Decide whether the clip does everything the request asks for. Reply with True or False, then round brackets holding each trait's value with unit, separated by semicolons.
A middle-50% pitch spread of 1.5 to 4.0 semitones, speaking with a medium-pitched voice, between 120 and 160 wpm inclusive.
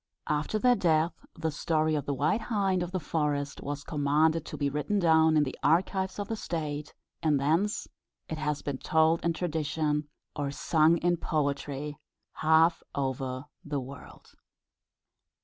True (2.5 semitones; 155 Hz; 155 wpm)